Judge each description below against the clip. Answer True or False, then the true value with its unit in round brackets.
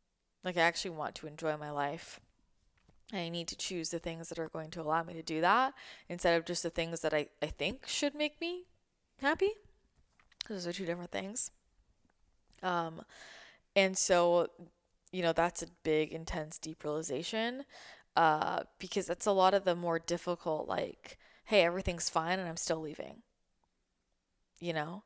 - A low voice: False (170 Hz)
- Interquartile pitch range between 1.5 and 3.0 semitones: True (2.5 semitones)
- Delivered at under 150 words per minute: False (170 wpm)